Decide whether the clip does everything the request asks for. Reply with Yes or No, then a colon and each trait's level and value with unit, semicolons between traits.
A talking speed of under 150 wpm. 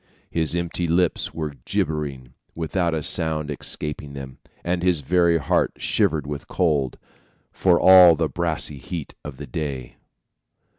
Yes: average, 140 wpm